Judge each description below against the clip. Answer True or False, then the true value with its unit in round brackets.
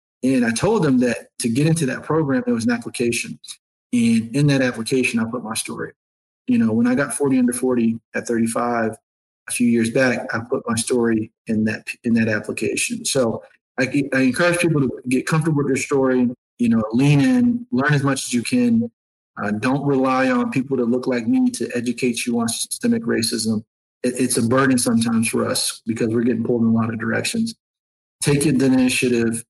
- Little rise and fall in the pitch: False (3.5 semitones)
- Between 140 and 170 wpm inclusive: False (205 wpm)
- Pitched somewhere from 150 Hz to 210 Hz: False (125 Hz)